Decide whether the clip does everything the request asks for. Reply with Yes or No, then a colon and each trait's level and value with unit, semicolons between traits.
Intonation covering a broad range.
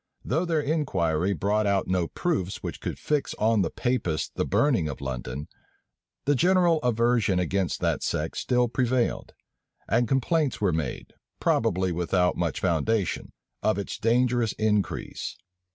Yes: wide, 5.9 semitones